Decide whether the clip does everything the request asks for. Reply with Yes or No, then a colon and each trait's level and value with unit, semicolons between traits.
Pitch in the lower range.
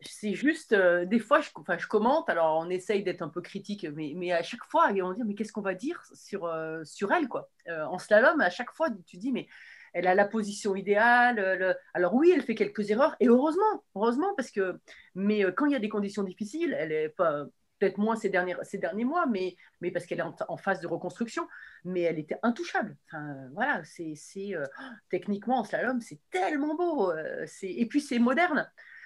No: high, 205 Hz